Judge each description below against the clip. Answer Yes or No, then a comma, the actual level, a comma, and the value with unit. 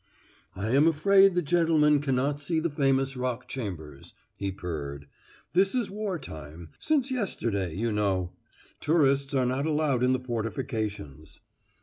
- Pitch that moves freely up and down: Yes, wide, 7.7 semitones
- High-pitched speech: No, low, 135 Hz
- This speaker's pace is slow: No, average, 145 wpm